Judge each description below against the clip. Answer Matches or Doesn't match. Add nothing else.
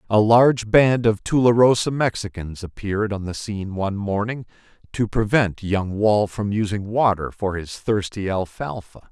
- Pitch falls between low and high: Doesn't match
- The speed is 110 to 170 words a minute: Matches